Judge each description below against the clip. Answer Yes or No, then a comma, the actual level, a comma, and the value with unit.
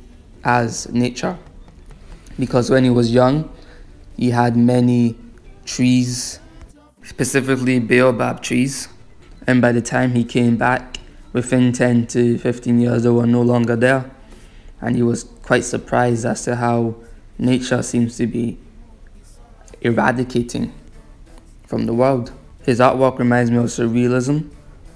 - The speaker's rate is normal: No, slow, 125 wpm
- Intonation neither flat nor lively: No, narrow, 1.2 semitones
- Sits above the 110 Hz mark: Yes, low, 120 Hz